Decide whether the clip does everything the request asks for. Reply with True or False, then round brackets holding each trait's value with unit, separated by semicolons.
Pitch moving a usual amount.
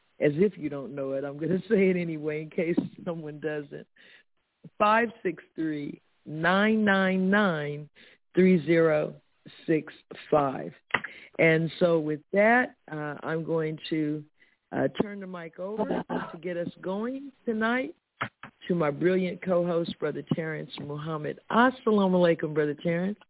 True (4.4 semitones)